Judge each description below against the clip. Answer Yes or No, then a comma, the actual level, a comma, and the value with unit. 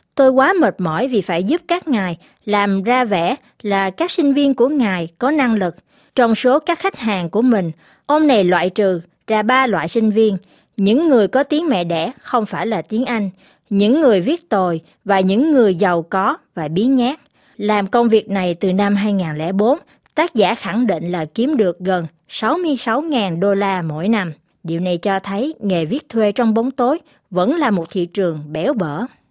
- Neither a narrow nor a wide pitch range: No, wide, 5.7 semitones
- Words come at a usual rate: Yes, average, 200 wpm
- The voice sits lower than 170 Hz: No, high, 210 Hz